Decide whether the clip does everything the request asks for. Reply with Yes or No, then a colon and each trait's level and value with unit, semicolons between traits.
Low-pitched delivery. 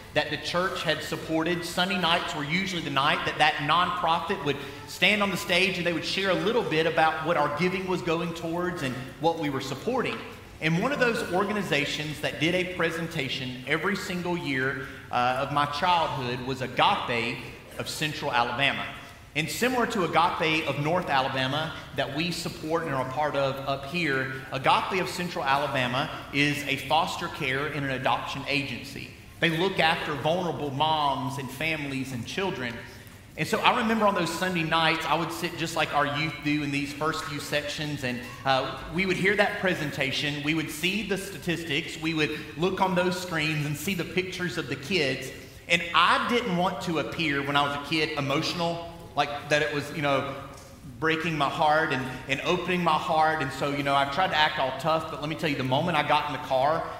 No: medium, 155 Hz